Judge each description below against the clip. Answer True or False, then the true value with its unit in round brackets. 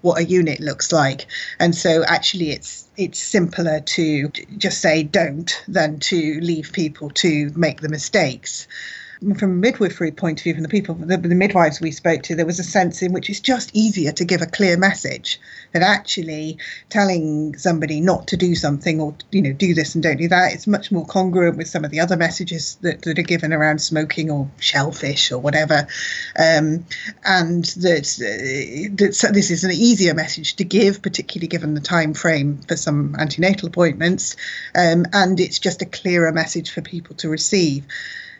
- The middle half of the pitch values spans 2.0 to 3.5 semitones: True (2.9 semitones)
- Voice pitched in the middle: True (170 Hz)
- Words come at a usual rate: True (190 wpm)